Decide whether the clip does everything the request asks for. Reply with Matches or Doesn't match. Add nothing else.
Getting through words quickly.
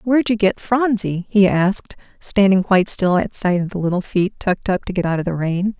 Matches